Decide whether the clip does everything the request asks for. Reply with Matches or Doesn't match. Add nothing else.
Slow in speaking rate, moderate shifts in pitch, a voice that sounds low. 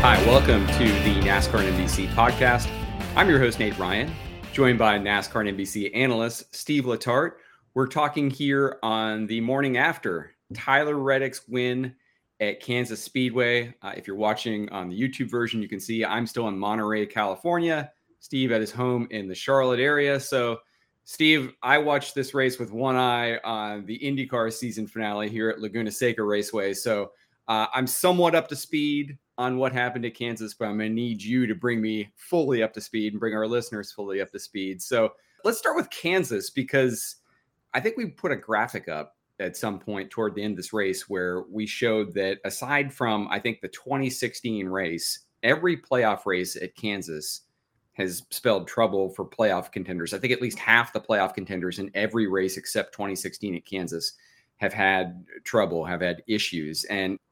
Doesn't match